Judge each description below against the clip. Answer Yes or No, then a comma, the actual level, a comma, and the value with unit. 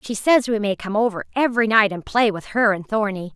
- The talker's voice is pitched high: Yes, high, 215 Hz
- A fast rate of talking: Yes, fast, 250 wpm